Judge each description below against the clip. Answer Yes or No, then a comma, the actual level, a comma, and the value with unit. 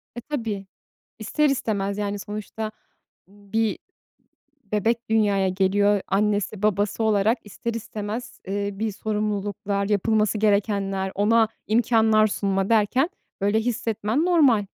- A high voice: Yes, high, 210 Hz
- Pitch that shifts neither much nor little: No, narrow, 1.8 semitones